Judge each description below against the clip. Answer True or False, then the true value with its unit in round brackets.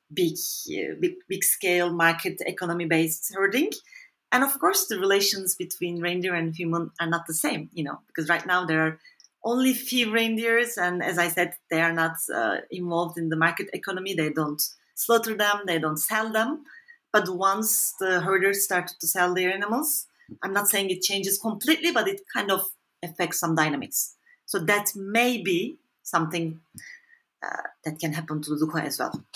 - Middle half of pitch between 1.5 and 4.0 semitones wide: False (5.1 semitones)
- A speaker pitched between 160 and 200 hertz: True (185 Hz)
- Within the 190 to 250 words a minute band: False (180 wpm)